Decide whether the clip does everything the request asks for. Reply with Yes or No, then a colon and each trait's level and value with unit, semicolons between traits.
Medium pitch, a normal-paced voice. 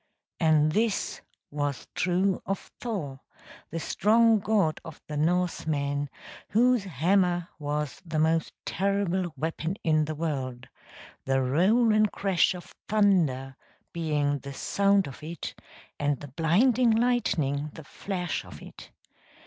No: medium, 165 Hz; slow, 125 wpm